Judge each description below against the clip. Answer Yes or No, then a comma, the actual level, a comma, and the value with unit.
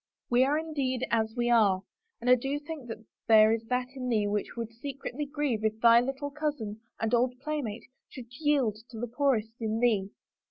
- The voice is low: No, high, 240 Hz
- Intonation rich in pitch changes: No, average, 3.7 semitones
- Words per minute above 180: Yes, average, 200 wpm